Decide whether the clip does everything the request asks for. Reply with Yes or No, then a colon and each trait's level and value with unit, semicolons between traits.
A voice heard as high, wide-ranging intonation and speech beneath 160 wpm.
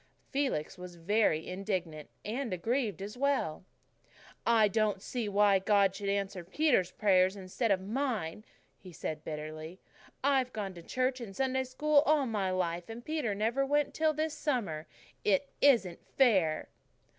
Yes: high, 205 Hz; wide, 5.9 semitones; average, 150 wpm